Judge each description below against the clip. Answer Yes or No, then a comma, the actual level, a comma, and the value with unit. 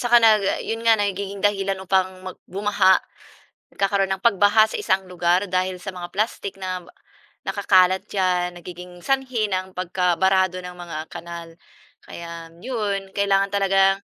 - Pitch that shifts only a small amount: Yes, narrow, 1.8 semitones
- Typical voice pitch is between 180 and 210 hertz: Yes, high, 190 Hz